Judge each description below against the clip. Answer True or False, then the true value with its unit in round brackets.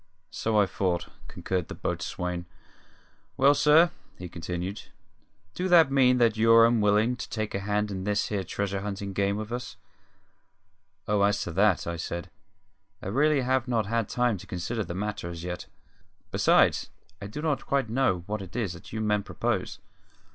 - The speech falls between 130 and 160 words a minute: False (175 wpm)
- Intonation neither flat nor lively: True (4.3 semitones)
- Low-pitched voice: True (105 Hz)